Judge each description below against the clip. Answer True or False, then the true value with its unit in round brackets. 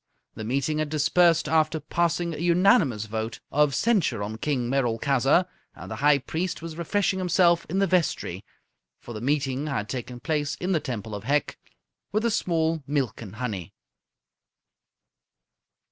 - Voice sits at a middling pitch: True (150 Hz)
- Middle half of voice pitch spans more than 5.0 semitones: True (5.5 semitones)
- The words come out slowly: False (155 wpm)